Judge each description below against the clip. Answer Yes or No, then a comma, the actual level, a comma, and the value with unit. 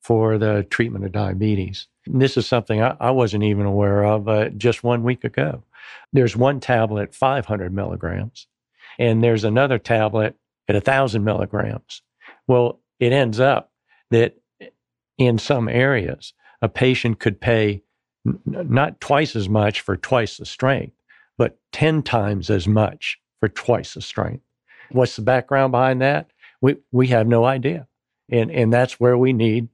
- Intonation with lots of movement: No, average, 3.2 semitones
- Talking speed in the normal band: Yes, average, 160 wpm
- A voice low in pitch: Yes, low, 115 Hz